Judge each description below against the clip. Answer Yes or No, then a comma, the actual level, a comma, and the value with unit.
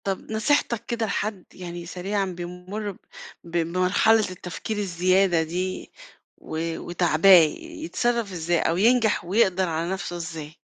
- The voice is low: No, medium, 185 Hz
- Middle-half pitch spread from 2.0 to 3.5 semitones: Yes, average, 3.2 semitones